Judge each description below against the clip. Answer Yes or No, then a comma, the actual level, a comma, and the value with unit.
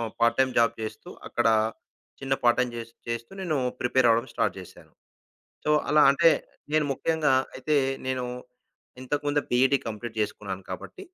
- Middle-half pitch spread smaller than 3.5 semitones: No, average, 3.8 semitones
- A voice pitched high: No, low, 125 Hz